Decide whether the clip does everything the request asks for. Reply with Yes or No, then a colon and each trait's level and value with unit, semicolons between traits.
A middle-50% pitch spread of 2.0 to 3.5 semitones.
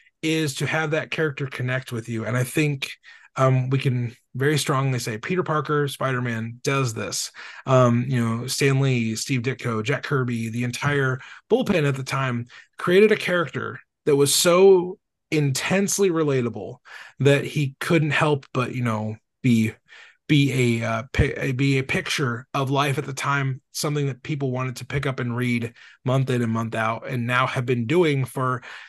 Yes: average, 3.2 semitones